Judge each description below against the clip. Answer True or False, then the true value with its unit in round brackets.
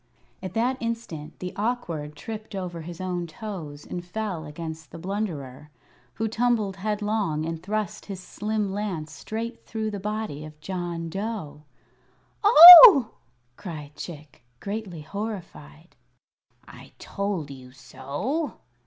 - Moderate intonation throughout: False (5.7 semitones)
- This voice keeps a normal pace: False (125 wpm)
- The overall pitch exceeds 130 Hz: True (185 Hz)